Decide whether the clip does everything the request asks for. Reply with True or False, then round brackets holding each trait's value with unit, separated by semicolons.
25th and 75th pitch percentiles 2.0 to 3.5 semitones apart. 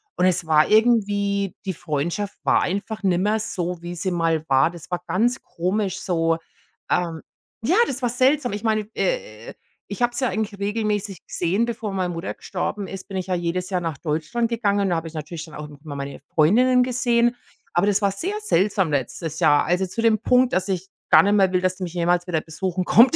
False (4.3 semitones)